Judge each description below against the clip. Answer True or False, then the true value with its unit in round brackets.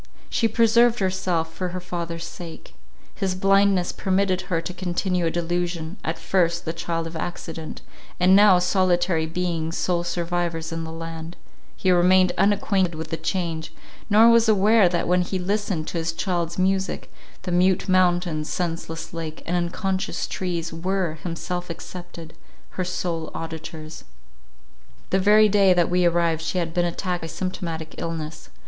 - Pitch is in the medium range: True (175 Hz)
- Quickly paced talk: False (155 wpm)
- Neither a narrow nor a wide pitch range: False (2.2 semitones)